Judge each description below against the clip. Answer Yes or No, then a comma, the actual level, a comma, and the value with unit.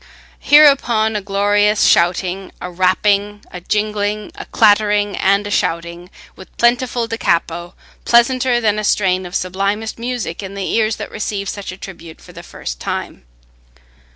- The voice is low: No, high, 205 Hz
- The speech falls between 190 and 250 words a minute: No, average, 155 wpm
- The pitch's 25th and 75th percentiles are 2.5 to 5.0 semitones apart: Yes, average, 2.8 semitones